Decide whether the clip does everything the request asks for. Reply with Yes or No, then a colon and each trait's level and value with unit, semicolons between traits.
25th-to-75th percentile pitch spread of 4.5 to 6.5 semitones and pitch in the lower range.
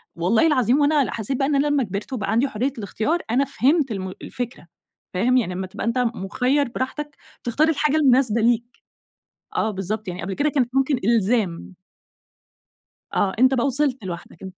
No: average, 5.0 semitones; high, 245 Hz